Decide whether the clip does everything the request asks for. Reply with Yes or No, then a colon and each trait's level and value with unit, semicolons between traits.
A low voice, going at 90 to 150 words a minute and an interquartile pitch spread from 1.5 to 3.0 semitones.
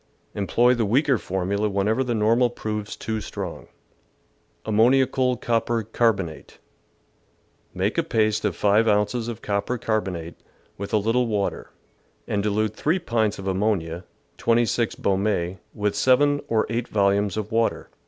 Yes: low, 110 Hz; average, 140 wpm; average, 2.7 semitones